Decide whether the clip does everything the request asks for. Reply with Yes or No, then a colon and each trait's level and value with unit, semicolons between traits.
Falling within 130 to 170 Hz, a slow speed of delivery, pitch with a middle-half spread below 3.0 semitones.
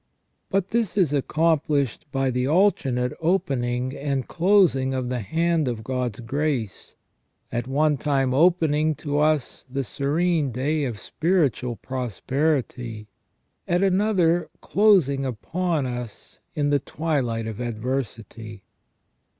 No: medium, 140 Hz; slow, 120 wpm; average, 4.6 semitones